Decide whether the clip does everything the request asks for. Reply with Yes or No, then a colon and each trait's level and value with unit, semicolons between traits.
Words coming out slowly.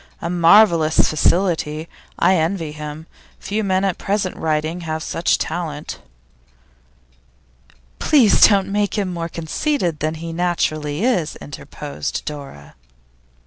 Yes: slow, 115 wpm